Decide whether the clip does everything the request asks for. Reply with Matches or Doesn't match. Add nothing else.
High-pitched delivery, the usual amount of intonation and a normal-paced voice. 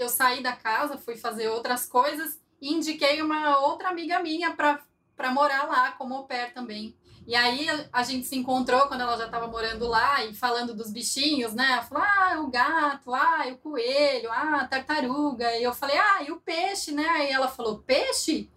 Doesn't match